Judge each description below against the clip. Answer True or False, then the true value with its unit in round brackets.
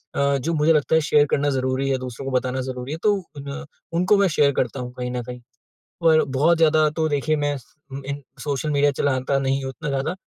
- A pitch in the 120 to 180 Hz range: True (140 Hz)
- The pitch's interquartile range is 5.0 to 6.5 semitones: False (2.7 semitones)